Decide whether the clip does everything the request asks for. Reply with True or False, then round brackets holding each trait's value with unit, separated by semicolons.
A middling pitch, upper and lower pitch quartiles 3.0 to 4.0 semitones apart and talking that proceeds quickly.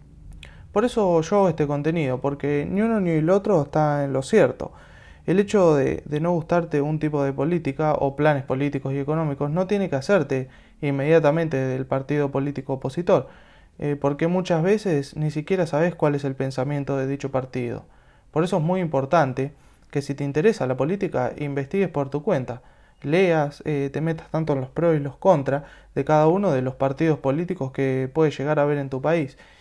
True (145 Hz; 3.5 semitones; 195 wpm)